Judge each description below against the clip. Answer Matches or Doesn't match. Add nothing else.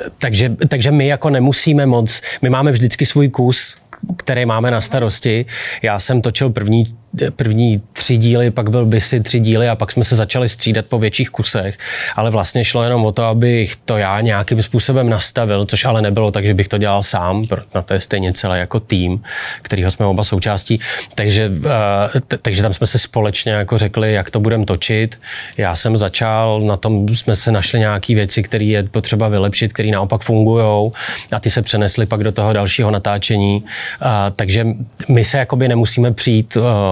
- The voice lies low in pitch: Matches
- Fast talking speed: Matches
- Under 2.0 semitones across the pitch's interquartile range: Doesn't match